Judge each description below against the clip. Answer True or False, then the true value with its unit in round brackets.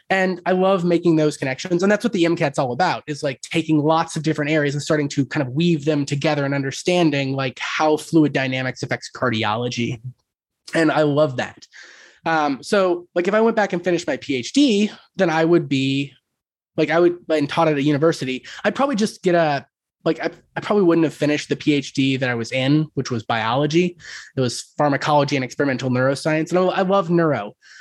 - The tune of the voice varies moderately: True (4.0 semitones)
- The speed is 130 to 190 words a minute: False (205 wpm)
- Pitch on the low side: False (155 Hz)